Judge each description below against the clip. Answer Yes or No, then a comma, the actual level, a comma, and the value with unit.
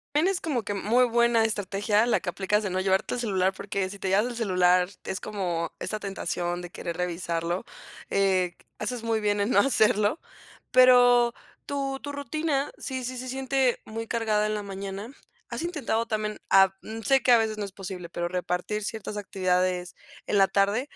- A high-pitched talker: Yes, high, 210 Hz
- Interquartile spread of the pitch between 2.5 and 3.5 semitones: No, average, 4.1 semitones